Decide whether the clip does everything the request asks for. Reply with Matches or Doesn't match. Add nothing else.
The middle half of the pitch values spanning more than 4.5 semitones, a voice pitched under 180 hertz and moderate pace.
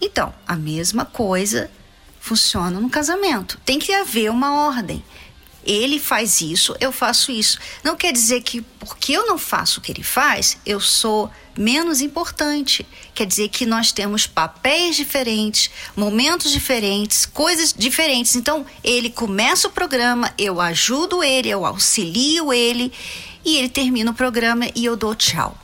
Doesn't match